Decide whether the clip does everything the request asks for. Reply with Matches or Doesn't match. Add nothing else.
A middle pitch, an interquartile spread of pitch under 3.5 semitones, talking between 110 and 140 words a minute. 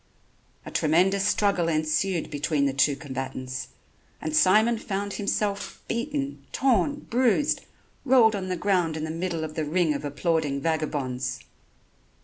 Doesn't match